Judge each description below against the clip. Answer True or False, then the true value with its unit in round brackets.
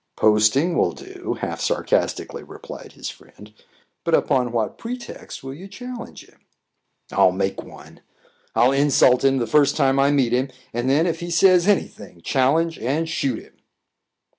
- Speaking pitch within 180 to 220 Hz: False (135 Hz)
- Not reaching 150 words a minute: False (165 wpm)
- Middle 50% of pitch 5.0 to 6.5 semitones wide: True (5.6 semitones)